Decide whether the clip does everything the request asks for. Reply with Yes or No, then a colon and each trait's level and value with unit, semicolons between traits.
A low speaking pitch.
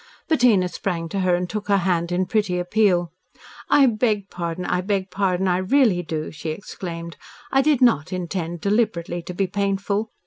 No: medium, 185 Hz